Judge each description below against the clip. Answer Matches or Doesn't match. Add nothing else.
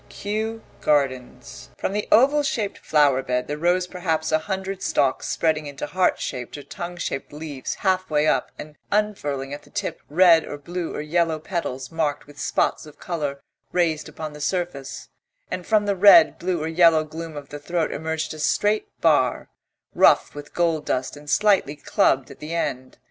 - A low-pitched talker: Doesn't match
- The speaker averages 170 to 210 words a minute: Matches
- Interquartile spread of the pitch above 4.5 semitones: Doesn't match